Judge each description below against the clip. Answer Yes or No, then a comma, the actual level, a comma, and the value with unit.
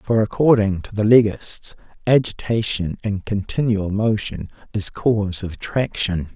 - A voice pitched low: Yes, low, 105 Hz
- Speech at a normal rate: No, slow, 125 wpm